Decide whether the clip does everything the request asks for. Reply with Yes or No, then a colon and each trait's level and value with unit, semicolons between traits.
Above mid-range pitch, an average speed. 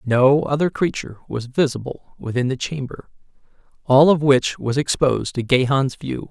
No: low, 135 Hz; average, 150 wpm